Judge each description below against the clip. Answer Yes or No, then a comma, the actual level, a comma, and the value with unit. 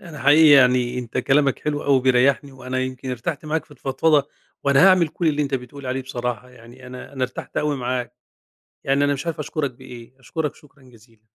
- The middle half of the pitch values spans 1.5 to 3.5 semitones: Yes, narrow, 2.6 semitones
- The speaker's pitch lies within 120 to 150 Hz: Yes, low, 135 Hz